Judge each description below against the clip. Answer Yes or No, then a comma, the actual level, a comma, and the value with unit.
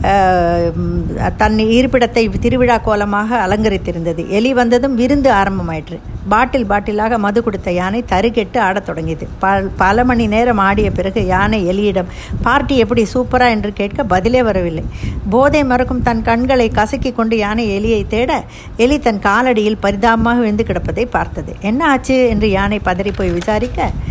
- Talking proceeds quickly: Yes, fast, 135 wpm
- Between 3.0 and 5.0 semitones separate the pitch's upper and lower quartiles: Yes, average, 3.8 semitones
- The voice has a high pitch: Yes, high, 220 Hz